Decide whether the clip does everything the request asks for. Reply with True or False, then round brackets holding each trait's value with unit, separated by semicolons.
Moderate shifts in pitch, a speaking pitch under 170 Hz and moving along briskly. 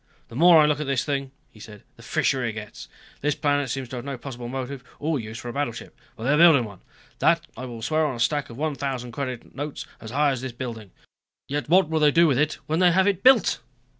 True (3.8 semitones; 135 Hz; 255 wpm)